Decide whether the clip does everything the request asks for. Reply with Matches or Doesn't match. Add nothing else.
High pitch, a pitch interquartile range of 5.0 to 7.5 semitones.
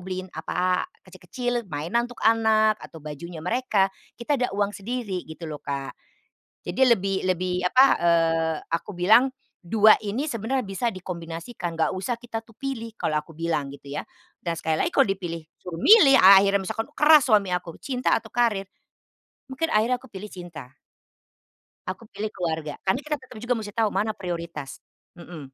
Matches